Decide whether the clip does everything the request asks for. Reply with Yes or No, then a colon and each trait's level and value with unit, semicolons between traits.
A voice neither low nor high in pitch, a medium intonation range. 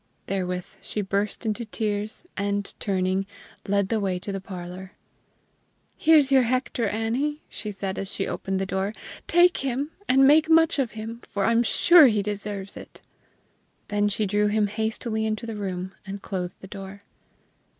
No: high, 210 Hz; average, 3.2 semitones